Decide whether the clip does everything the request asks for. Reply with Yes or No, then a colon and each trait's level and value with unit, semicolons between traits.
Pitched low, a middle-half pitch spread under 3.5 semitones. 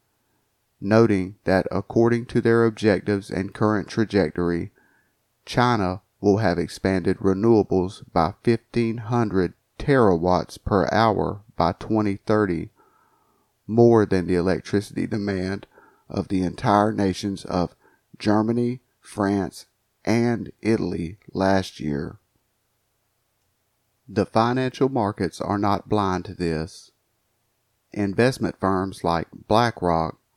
Yes: low, 105 Hz; average, 3.1 semitones